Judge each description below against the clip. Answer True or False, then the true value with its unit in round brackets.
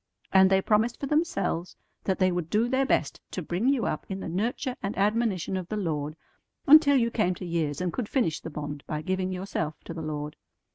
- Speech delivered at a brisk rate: True (220 wpm)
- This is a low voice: False (190 Hz)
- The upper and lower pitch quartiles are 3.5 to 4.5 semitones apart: False (5.6 semitones)